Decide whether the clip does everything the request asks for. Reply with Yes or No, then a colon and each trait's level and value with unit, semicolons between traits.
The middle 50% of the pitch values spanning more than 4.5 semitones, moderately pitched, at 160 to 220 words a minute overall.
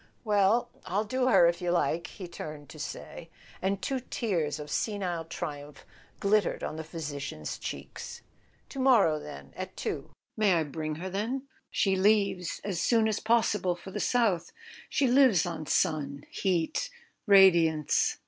No: average, 5.0 semitones; medium, 180 Hz; average, 150 wpm